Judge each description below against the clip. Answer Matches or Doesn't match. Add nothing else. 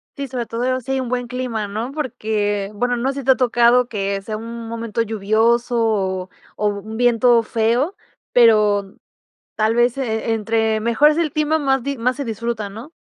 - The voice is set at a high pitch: Matches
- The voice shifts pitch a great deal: Doesn't match